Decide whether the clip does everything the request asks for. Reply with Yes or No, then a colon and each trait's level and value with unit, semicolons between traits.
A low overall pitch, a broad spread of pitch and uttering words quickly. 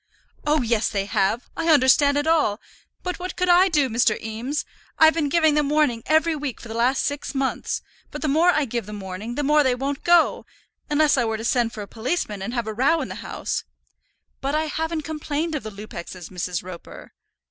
No: very high, 275 Hz; wide, 5.7 semitones; fast, 220 wpm